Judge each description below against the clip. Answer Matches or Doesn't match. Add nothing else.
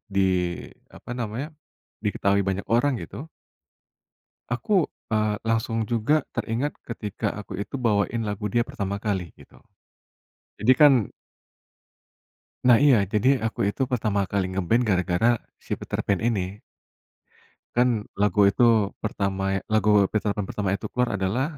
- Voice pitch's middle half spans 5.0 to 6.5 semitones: Doesn't match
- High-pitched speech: Doesn't match